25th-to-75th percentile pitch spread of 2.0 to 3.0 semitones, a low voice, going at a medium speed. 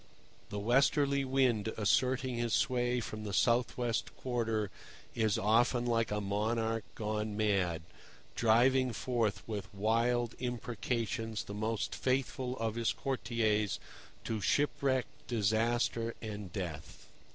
No: narrow, 2.5 semitones; low, 115 Hz; slow, 120 wpm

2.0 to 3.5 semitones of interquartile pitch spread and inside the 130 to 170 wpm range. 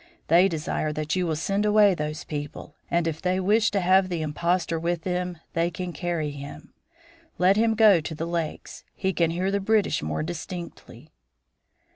No: average, 3.2 semitones; average, 180 wpm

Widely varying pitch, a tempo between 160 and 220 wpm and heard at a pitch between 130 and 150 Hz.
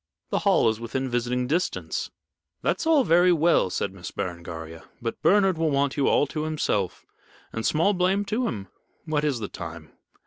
Yes: wide, 8.5 semitones; average, 175 wpm; medium, 140 Hz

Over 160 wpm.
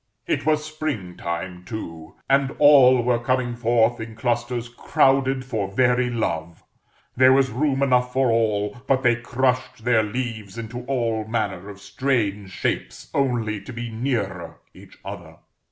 No: average, 150 wpm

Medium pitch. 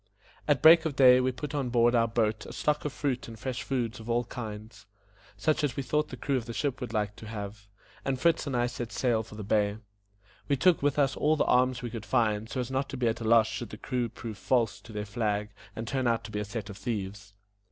No: low, 120 Hz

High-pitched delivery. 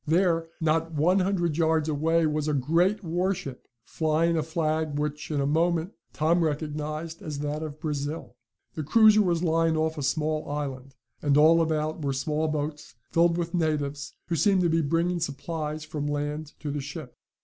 No: medium, 155 Hz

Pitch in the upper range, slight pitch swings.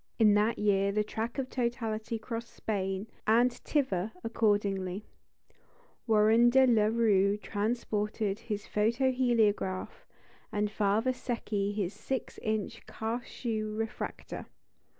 Yes: high, 215 Hz; narrow, 2.3 semitones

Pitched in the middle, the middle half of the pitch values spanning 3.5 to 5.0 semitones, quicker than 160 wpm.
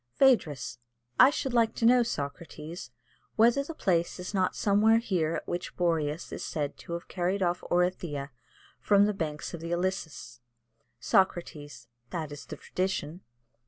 No: medium, 175 Hz; average, 4.6 semitones; average, 155 wpm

